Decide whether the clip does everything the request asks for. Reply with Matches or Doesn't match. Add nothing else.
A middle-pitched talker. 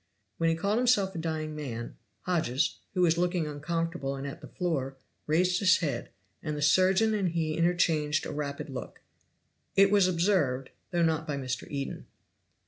Matches